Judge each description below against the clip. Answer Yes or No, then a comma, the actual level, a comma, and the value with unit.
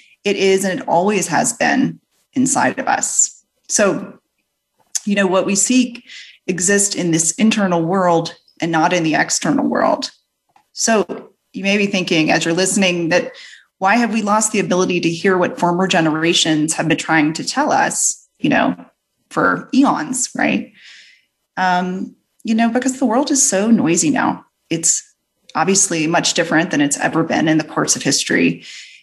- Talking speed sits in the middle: Yes, average, 165 wpm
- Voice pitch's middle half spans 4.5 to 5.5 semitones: Yes, average, 5.1 semitones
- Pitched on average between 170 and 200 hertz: Yes, high, 190 Hz